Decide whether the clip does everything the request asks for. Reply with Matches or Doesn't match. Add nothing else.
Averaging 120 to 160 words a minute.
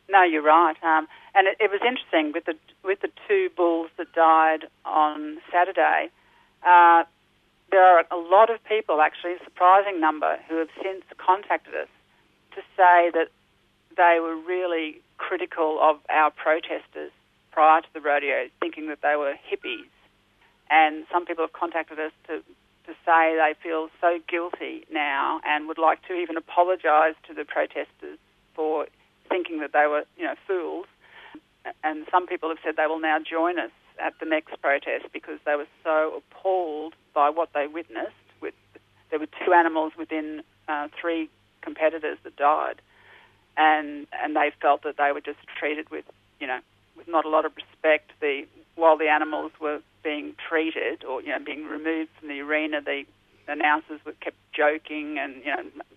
Doesn't match